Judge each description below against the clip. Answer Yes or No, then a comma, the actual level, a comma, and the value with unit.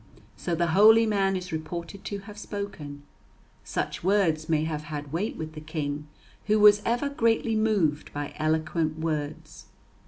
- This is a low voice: No, medium, 170 Hz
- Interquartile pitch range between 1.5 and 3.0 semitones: No, average, 5.1 semitones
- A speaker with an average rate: Yes, average, 155 wpm